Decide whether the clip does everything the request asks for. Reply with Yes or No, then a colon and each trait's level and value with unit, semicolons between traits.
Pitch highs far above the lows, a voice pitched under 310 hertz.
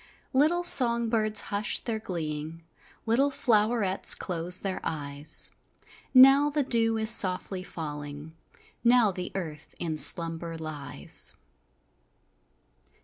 Yes: wide, 6.5 semitones; high, 190 Hz